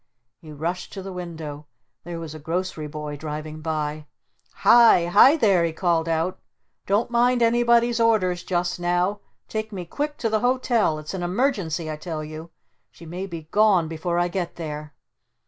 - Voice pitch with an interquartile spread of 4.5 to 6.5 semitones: Yes, average, 5.0 semitones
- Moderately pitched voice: Yes, medium, 175 Hz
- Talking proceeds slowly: No, average, 170 wpm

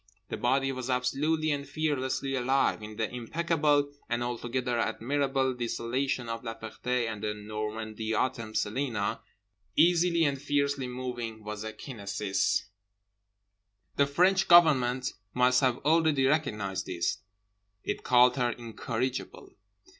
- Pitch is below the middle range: Yes, low, 125 Hz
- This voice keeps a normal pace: No, slow, 125 wpm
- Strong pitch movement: No, average, 3.9 semitones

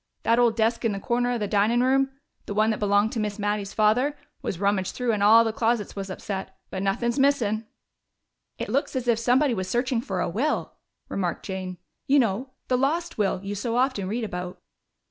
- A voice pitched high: Yes, high, 220 Hz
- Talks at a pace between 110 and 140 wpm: No, fast, 205 wpm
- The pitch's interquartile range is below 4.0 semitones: Yes, average, 3.5 semitones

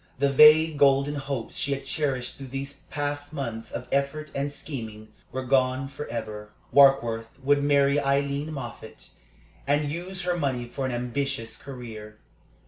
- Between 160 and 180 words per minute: No, average, 145 wpm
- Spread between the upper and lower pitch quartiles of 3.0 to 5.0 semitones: No, narrow, 2.6 semitones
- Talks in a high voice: No, medium, 140 Hz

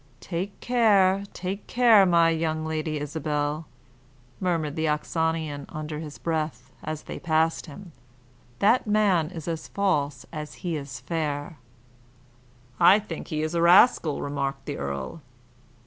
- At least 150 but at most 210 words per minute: No, slow, 135 wpm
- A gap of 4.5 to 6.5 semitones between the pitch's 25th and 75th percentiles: No, average, 3.3 semitones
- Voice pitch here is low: No, medium, 160 Hz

